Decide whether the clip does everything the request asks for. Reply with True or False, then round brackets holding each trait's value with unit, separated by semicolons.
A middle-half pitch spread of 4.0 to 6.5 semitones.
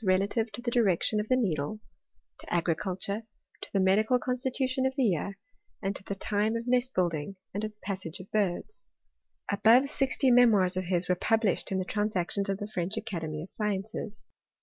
False (3.6 semitones)